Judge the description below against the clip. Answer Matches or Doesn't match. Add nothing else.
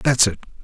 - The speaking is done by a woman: Doesn't match